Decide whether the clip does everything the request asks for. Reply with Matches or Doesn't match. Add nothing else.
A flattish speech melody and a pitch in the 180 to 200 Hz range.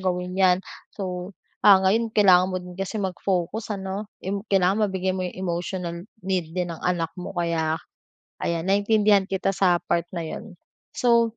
Matches